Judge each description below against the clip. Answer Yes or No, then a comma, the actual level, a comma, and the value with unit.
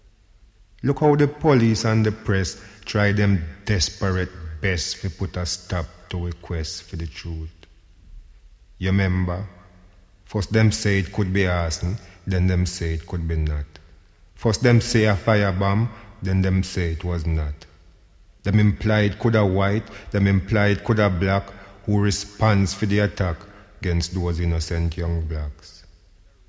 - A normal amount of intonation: Yes, average, 3.2 semitones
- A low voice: Yes, very low, 95 Hz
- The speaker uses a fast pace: No, average, 155 wpm